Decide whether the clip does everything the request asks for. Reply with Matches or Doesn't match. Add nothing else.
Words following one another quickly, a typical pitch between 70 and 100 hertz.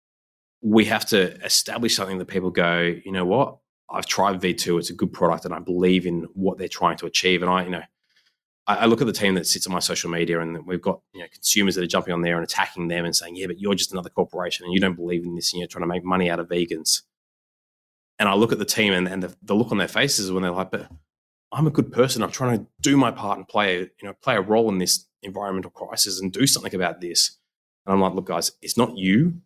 Matches